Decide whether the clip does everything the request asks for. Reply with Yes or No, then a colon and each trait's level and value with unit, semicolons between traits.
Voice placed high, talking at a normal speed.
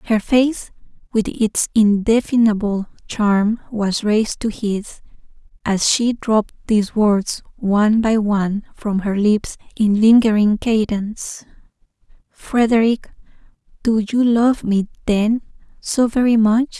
No: high, 215 Hz; slow, 115 wpm